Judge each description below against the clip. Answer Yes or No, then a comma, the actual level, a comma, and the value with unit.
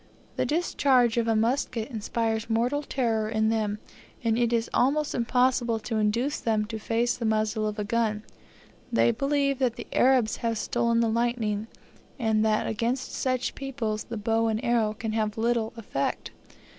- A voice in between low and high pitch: No, high, 230 Hz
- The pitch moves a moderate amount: No, narrow, 2.0 semitones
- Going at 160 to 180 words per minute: Yes, average, 170 wpm